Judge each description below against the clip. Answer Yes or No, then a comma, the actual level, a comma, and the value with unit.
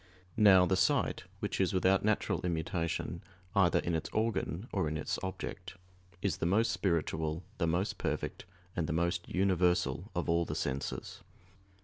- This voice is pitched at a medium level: No, very low, 90 Hz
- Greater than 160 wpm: No, average, 155 wpm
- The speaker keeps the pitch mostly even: Yes, narrow, 2.3 semitones